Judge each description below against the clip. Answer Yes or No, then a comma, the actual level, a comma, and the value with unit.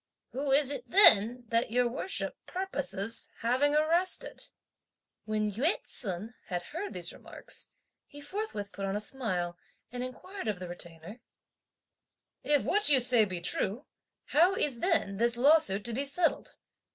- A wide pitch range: Yes, wide, 6.5 semitones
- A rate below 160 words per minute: Yes, average, 150 wpm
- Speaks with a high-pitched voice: Yes, high, 245 Hz